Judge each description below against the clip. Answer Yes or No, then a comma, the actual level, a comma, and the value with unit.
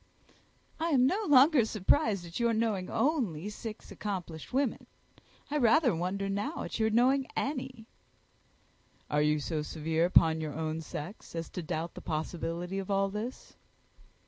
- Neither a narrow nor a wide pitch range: No, wide, 7.1 semitones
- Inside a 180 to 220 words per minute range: No, average, 150 wpm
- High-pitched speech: Yes, high, 195 Hz